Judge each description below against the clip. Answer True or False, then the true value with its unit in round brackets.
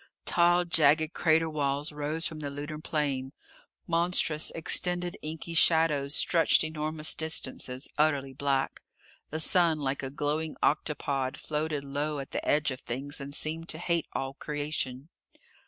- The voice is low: False (150 Hz)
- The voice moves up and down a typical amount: False (2.2 semitones)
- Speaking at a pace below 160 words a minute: True (140 wpm)